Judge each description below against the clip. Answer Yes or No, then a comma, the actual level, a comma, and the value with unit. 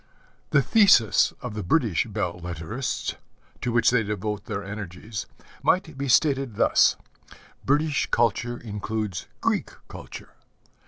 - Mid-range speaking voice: No, low, 110 Hz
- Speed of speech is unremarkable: No, slow, 120 wpm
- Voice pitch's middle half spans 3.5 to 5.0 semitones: Yes, average, 4.3 semitones